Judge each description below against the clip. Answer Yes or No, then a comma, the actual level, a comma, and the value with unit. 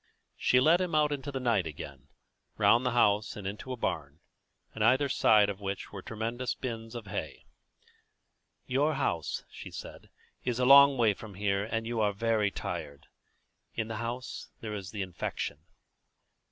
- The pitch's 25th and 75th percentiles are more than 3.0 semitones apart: Yes, average, 4.0 semitones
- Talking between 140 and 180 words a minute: Yes, average, 175 wpm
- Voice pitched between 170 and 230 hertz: No, low, 115 Hz